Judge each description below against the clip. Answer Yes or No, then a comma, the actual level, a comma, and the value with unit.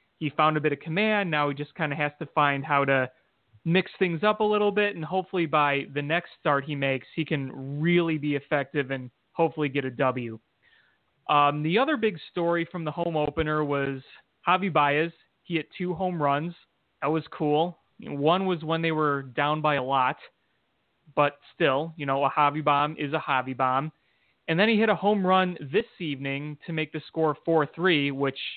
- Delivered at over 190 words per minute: Yes, average, 200 wpm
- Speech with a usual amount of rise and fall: Yes, average, 3.0 semitones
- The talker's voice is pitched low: No, medium, 150 Hz